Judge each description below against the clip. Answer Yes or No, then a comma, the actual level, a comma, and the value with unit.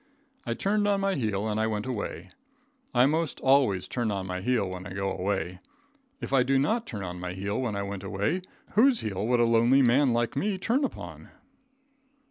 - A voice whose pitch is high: No, low, 115 Hz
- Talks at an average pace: No, fast, 210 wpm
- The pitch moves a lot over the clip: Yes, wide, 5.9 semitones